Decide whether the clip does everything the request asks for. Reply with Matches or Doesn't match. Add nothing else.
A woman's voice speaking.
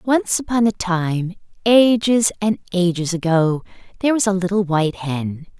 Matches